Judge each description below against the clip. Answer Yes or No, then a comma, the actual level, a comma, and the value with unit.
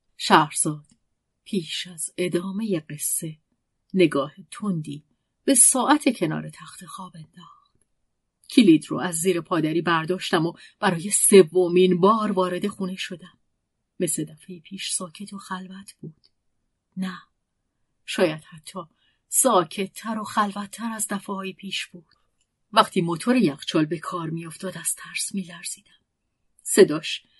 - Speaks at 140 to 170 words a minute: No, average, 125 wpm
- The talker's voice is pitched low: No, medium, 185 Hz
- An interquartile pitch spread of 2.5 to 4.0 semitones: Yes, average, 3.0 semitones